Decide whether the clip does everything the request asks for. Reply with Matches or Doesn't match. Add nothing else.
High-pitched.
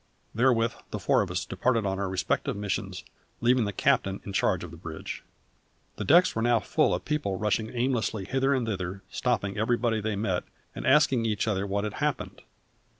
Doesn't match